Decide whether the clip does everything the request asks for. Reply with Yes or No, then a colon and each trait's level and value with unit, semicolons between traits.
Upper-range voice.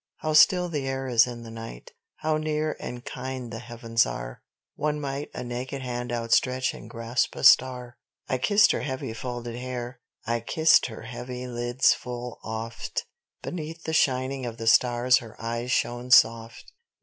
No: low, 125 Hz